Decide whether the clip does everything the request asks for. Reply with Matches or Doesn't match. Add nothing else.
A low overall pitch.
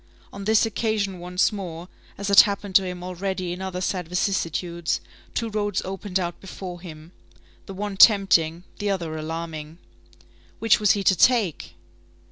Doesn't match